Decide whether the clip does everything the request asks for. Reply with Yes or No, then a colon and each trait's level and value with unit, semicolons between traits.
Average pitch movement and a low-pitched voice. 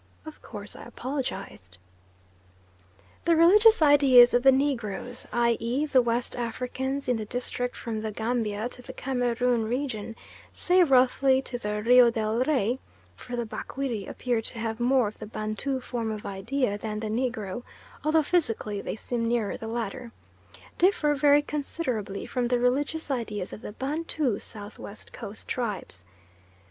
No: average, 3.6 semitones; high, 245 Hz